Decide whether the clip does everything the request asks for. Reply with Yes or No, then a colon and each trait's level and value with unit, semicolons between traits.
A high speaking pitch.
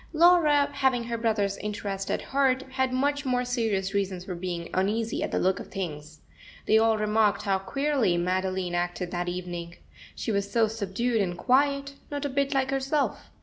Yes: high, 215 Hz